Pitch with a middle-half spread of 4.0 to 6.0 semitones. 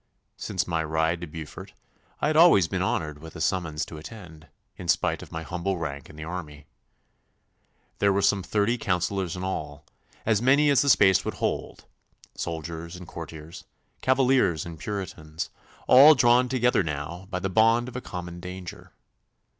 Yes: average, 4.9 semitones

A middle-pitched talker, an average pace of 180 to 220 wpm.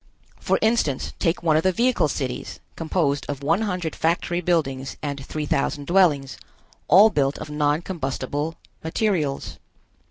No: medium, 155 Hz; average, 140 wpm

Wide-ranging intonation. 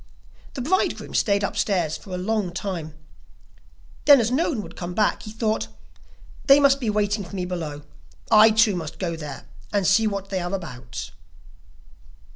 No: average, 3.8 semitones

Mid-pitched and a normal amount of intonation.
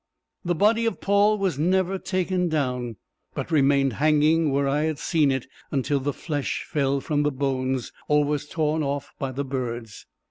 Yes: medium, 145 Hz; average, 3.3 semitones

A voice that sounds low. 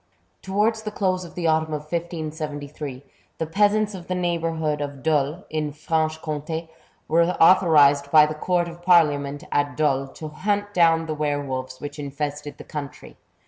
No: medium, 155 Hz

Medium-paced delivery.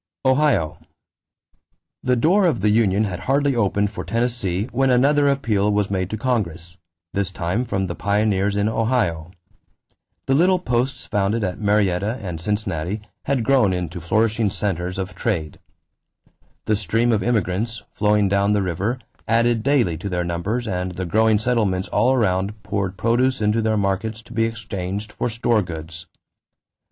Yes: average, 155 wpm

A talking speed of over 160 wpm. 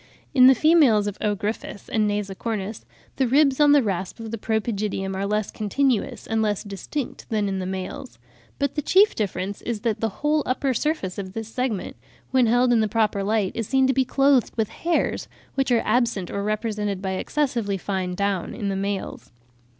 Yes: average, 200 wpm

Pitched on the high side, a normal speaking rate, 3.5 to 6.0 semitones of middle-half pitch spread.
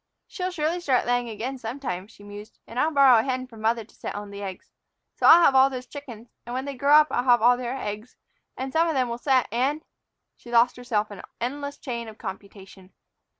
No: high, 245 Hz; fast, 240 wpm; average, 3.8 semitones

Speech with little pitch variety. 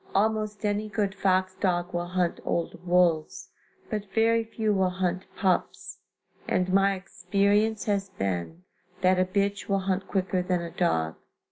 Yes: narrow, 2.1 semitones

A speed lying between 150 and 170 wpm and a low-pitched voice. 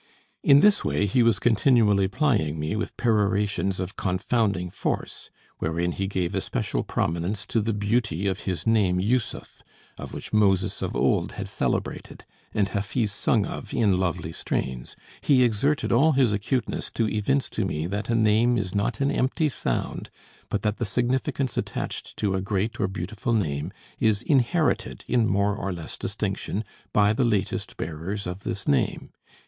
Yes: average, 165 wpm; low, 105 Hz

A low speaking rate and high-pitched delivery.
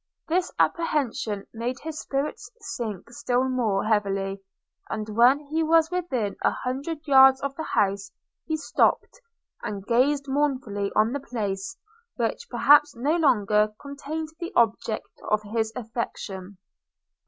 Yes: slow, 130 wpm; very high, 250 Hz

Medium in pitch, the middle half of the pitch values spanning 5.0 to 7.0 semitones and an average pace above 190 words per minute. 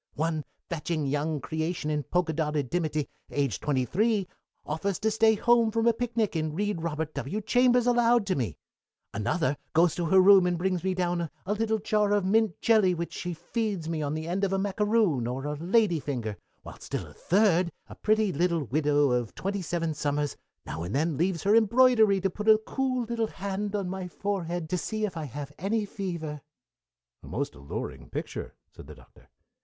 Yes: medium, 175 Hz; wide, 5.5 semitones; average, 200 wpm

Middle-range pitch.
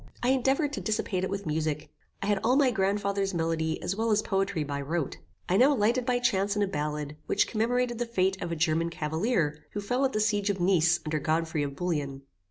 No: high, 195 Hz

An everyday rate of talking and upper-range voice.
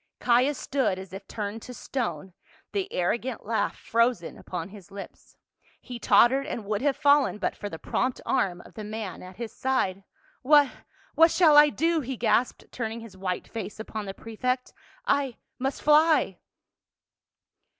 Yes: average, 170 wpm; high, 230 Hz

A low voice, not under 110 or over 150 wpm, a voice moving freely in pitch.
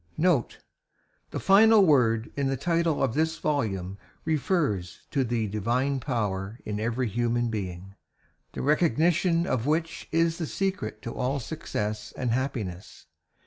Yes: low, 130 Hz; average, 140 wpm; wide, 6.8 semitones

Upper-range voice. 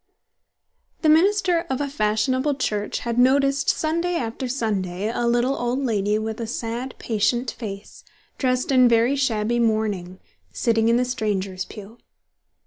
Yes: high, 235 Hz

